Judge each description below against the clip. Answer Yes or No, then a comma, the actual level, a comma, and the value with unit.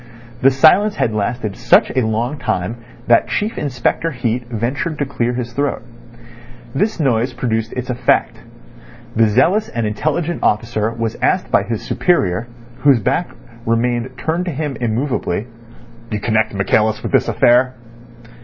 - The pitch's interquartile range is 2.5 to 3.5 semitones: No, average, 4.0 semitones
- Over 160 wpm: No, average, 145 wpm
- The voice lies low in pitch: Yes, low, 120 Hz